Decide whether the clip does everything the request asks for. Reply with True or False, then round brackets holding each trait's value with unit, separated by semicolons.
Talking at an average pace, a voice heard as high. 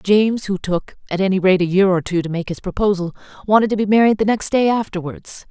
False (240 wpm; 195 Hz)